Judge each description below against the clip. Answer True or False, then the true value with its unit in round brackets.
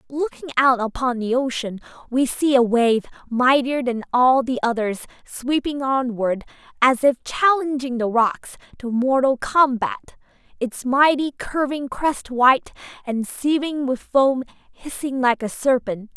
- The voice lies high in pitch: True (255 Hz)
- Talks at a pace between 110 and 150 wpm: True (135 wpm)